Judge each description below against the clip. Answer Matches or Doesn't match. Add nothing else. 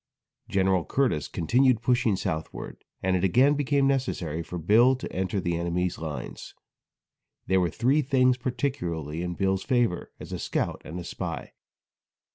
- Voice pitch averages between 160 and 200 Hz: Doesn't match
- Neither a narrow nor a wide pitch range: Doesn't match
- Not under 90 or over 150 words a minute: Matches